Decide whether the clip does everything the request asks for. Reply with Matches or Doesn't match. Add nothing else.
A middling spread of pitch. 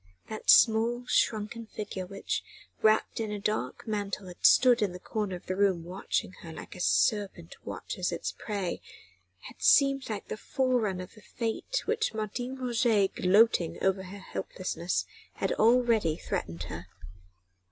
Matches